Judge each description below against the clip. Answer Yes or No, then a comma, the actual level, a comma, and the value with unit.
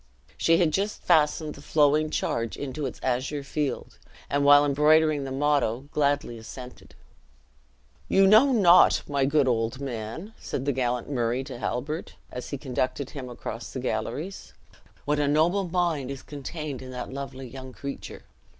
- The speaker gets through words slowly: No, average, 160 wpm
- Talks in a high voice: No, medium, 140 Hz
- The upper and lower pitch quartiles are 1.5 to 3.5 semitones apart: Yes, average, 3.1 semitones